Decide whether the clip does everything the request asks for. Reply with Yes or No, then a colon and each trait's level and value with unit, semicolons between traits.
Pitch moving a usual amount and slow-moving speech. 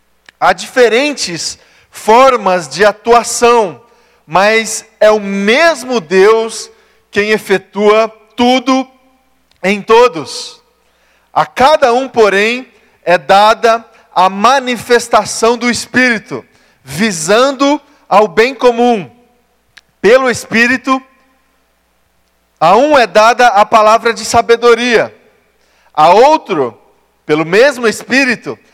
Yes: average, 3.2 semitones; slow, 90 wpm